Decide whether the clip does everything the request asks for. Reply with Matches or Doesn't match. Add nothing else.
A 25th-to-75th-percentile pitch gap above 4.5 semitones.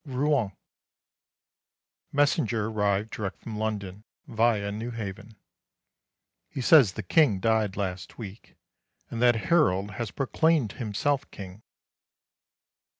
Doesn't match